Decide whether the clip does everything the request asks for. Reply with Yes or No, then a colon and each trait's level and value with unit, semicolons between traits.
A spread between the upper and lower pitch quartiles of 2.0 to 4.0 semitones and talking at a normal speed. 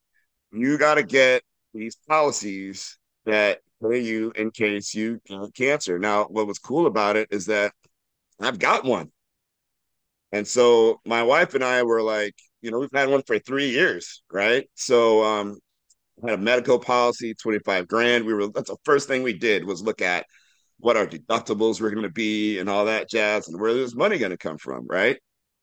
Yes: average, 2.8 semitones; average, 185 wpm